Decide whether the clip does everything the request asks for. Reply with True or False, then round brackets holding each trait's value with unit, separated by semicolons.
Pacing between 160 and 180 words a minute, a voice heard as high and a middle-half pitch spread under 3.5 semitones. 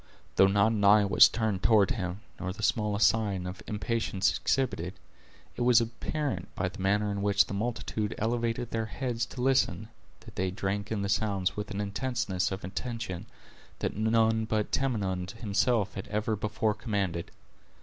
False (170 wpm; 105 Hz; 2.6 semitones)